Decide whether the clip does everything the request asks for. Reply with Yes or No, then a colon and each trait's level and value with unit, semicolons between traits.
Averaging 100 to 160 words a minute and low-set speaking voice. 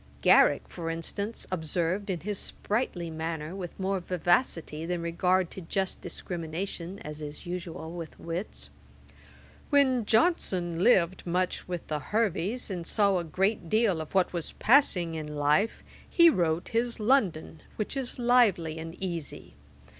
No: average, 145 wpm; medium, 180 Hz